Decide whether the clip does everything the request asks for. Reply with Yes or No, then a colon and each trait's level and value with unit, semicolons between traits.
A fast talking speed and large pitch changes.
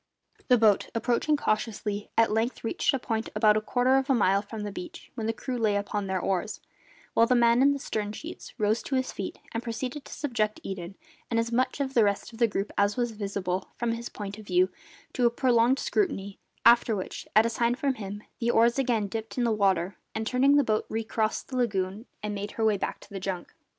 No: fast, 230 wpm; average, 3.0 semitones